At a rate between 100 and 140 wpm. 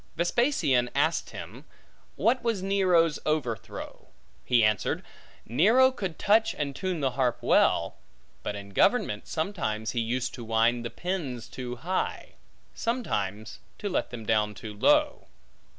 Yes: slow, 135 wpm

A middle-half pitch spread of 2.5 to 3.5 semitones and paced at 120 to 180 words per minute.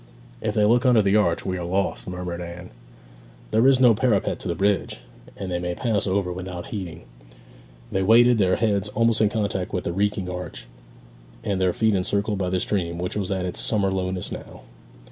No: average, 2.8 semitones; average, 200 wpm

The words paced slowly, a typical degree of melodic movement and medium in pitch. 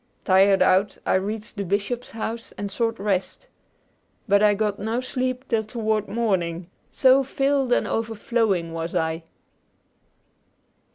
No: slow, 130 wpm; average, 3.4 semitones; high, 215 Hz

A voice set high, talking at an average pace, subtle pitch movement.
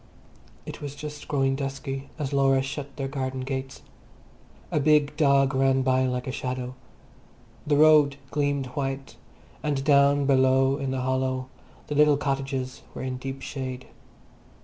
No: low, 135 Hz; average, 150 wpm; narrow, 1.3 semitones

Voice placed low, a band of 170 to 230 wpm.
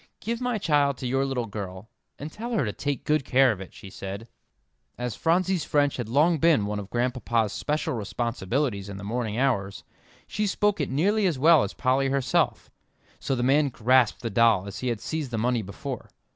Yes: low, 130 Hz; average, 200 wpm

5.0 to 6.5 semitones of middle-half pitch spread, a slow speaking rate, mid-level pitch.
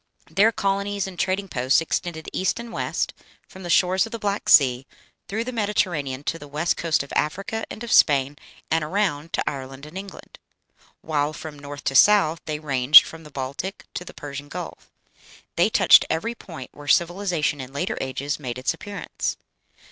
No: wide, 5.5 semitones; average, 180 wpm; medium, 160 Hz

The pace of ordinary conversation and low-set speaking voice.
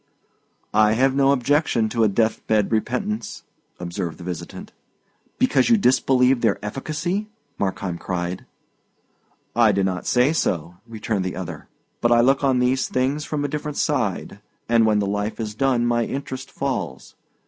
Yes: average, 160 wpm; low, 120 Hz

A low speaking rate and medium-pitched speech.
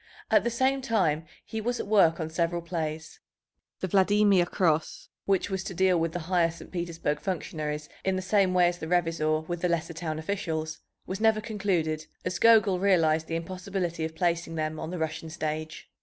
No: average, 190 wpm; medium, 175 Hz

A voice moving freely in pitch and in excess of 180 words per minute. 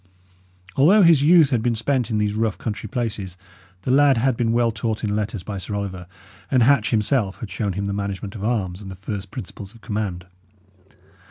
No: average, 3.4 semitones; average, 200 wpm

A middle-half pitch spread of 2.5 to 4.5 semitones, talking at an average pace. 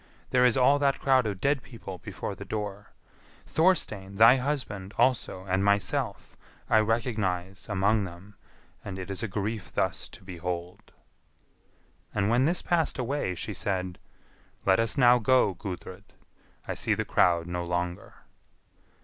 No: average, 5.1 semitones; average, 150 wpm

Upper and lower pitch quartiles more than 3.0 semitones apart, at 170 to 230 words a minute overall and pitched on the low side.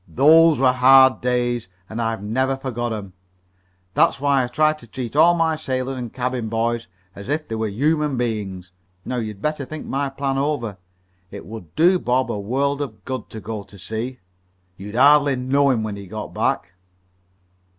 Yes: average, 4.1 semitones; average, 180 wpm; low, 125 Hz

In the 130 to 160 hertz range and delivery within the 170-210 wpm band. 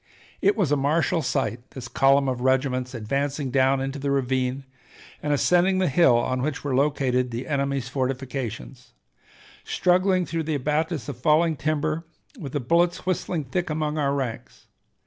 No: medium, 140 Hz; average, 160 wpm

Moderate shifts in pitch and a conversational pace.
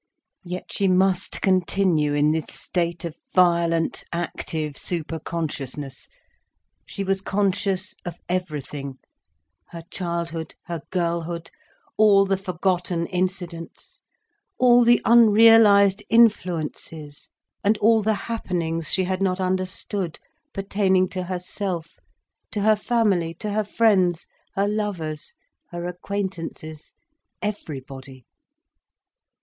No: average, 3.3 semitones; slow, 100 wpm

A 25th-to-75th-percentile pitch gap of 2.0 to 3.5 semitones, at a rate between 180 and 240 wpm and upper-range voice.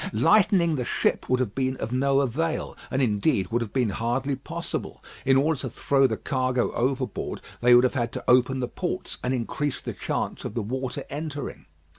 No: narrow, 2.6 semitones; average, 195 wpm; low, 130 Hz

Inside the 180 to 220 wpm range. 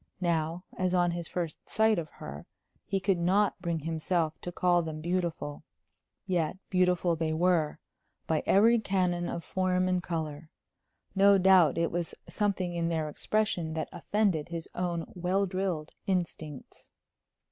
No: average, 145 wpm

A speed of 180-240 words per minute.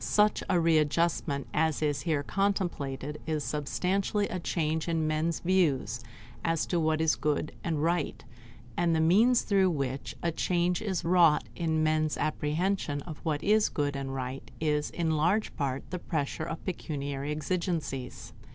No: average, 155 wpm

